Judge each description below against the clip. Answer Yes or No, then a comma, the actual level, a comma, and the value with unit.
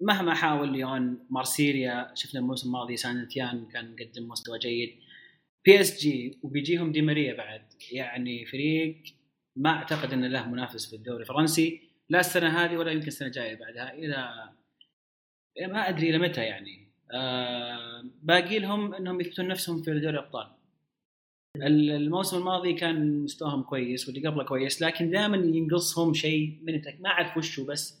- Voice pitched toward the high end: No, medium, 145 Hz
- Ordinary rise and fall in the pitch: Yes, average, 4.6 semitones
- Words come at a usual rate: No, fast, 145 wpm